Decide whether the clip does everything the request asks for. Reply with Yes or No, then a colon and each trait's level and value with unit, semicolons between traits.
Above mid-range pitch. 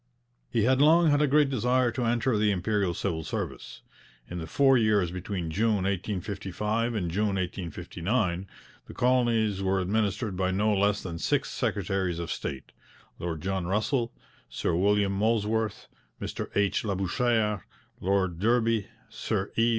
No: low, 105 Hz